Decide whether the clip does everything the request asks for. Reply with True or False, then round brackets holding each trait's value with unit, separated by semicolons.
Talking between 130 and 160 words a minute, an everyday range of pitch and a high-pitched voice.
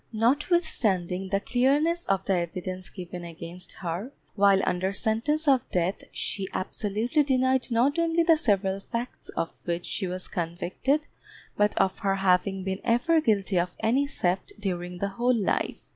False (155 wpm; 5.7 semitones; 200 Hz)